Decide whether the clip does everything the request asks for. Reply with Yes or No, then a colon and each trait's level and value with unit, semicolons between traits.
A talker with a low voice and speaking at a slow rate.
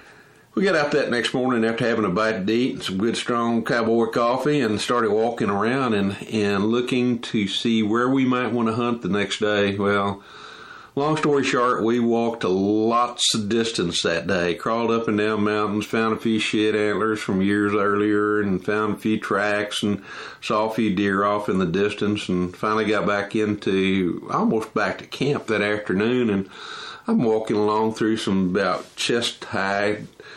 No: low, 110 Hz; average, 190 wpm